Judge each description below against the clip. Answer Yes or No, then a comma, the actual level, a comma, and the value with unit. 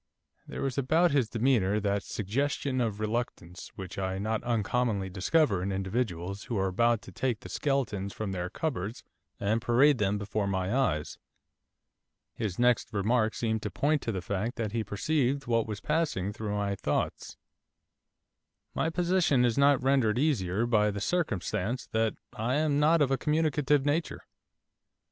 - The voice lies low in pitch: Yes, low, 115 Hz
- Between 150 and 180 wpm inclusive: Yes, average, 160 wpm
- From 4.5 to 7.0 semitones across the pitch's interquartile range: Yes, average, 5.3 semitones